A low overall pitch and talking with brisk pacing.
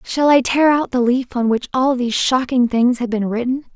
No: very high, 250 Hz; fast, 240 wpm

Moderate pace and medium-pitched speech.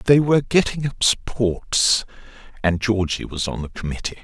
No: average, 155 wpm; low, 110 Hz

